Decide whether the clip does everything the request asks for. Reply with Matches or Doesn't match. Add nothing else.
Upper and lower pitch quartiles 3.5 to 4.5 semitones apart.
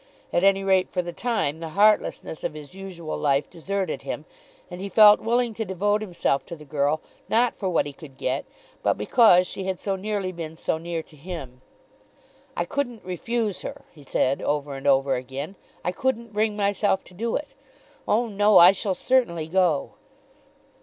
Doesn't match